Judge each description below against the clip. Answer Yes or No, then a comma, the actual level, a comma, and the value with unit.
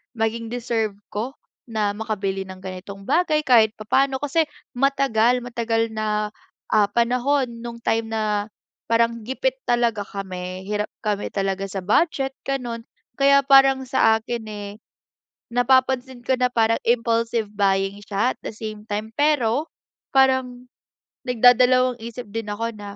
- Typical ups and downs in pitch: Yes, average, 3.2 semitones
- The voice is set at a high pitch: Yes, high, 230 Hz